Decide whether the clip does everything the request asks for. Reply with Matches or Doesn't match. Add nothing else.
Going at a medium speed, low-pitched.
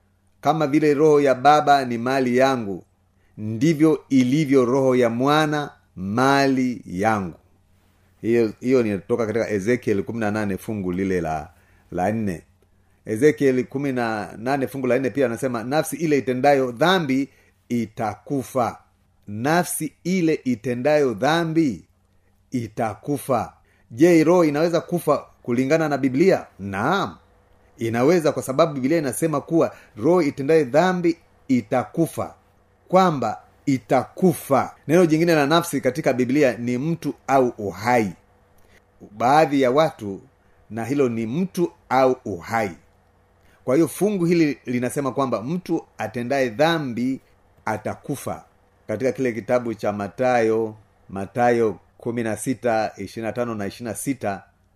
Matches